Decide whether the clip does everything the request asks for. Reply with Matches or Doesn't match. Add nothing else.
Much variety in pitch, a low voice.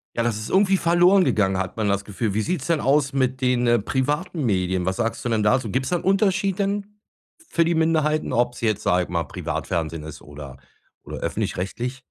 Matches